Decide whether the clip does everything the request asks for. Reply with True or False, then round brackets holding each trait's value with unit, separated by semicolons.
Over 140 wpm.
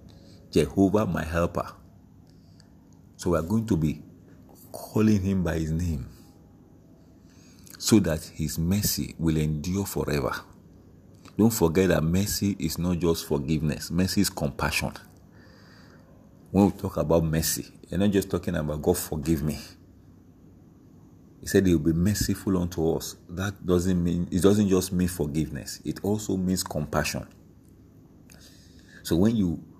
False (135 wpm)